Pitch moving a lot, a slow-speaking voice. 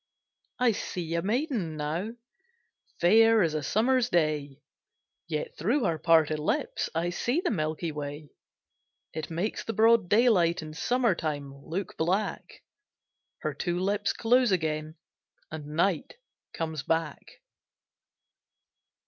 Yes: wide, 6.0 semitones; slow, 125 wpm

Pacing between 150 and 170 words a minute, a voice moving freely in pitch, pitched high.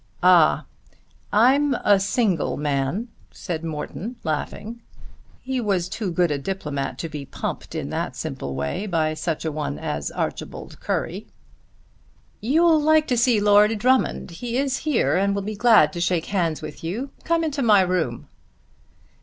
Yes: average, 155 wpm; wide, 7.2 semitones; high, 195 Hz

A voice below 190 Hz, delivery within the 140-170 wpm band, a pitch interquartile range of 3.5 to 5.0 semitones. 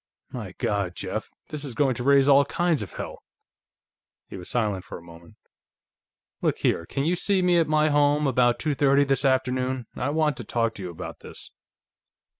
No: low, 135 Hz; average, 195 wpm; average, 4.3 semitones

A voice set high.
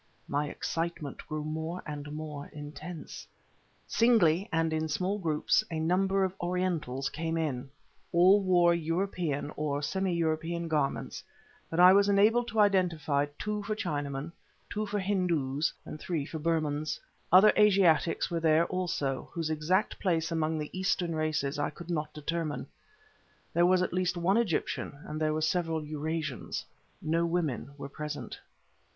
No: medium, 165 Hz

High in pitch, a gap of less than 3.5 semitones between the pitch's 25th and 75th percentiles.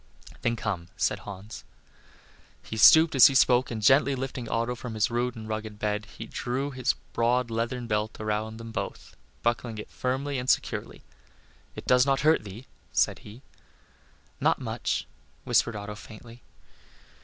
No: low, 115 Hz; average, 2.7 semitones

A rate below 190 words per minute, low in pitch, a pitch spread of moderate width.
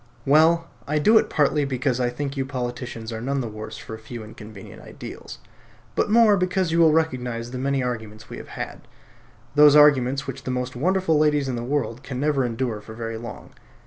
No: fast, 205 wpm; low, 130 Hz; average, 4.0 semitones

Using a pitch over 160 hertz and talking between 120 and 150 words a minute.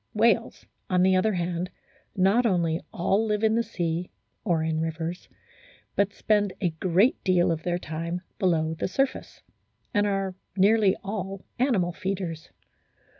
Yes: medium, 185 Hz; average, 145 wpm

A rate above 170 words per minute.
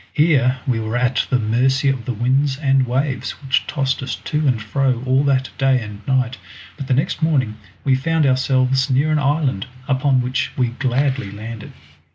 Yes: average, 185 wpm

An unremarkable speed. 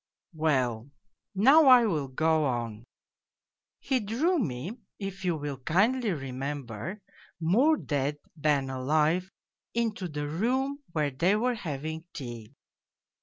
No: slow, 120 wpm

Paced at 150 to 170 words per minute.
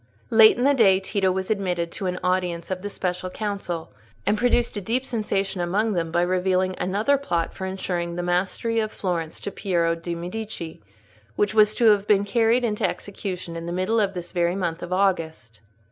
No: average, 195 wpm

